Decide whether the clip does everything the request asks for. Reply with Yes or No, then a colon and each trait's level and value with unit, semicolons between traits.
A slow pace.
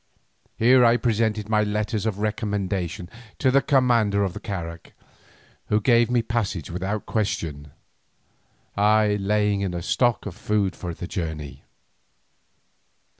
Yes: slow, 130 wpm